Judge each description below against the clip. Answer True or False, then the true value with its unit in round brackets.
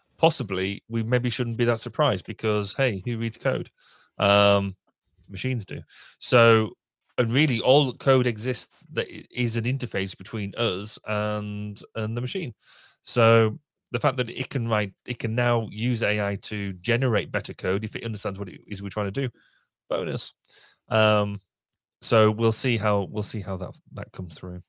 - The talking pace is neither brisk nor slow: True (170 wpm)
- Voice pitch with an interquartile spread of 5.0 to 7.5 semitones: False (3.3 semitones)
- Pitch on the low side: True (110 Hz)